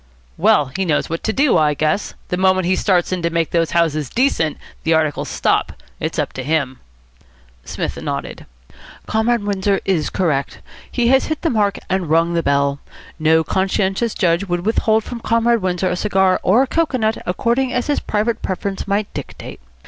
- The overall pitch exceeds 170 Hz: Yes, high, 190 Hz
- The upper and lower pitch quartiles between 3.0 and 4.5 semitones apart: No, average, 5.1 semitones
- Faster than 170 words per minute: Yes, average, 180 wpm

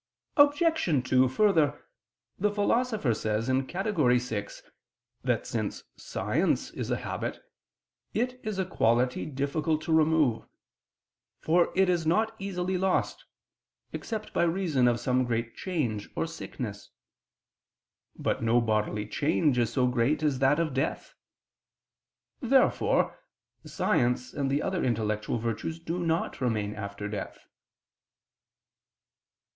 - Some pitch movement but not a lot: No, wide, 7.1 semitones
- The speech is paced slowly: Yes, slow, 120 wpm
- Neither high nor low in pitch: Yes, medium, 145 Hz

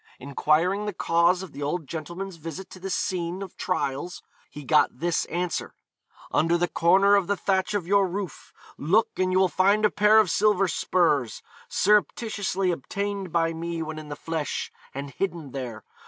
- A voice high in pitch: No, medium, 175 Hz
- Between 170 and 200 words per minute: Yes, average, 175 wpm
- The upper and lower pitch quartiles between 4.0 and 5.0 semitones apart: No, average, 3.5 semitones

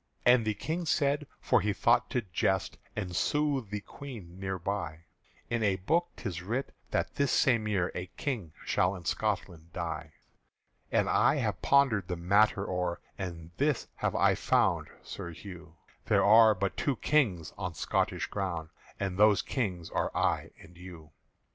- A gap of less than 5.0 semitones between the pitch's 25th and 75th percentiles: No, average, 5.3 semitones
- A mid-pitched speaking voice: No, low, 100 Hz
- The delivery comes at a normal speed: Yes, average, 160 wpm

